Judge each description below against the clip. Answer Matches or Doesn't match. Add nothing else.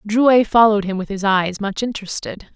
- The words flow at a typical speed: Matches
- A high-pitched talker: Matches